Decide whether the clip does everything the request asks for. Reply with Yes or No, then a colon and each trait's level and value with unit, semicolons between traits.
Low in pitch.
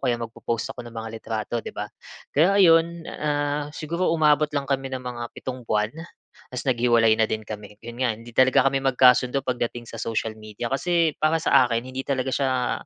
Yes: low, 125 Hz